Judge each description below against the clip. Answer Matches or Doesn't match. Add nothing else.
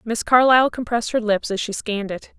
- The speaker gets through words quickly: Matches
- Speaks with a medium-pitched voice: Doesn't match